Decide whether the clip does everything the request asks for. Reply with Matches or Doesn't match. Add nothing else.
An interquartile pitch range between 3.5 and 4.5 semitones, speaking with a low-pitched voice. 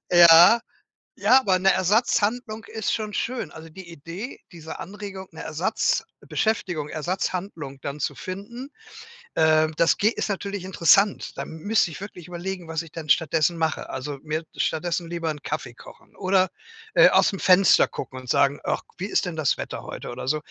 Doesn't match